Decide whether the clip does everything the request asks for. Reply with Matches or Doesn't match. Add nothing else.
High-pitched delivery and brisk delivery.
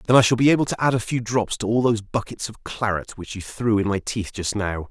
Doesn't match